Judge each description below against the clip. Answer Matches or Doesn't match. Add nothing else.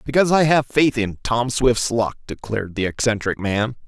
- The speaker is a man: Matches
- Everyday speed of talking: Matches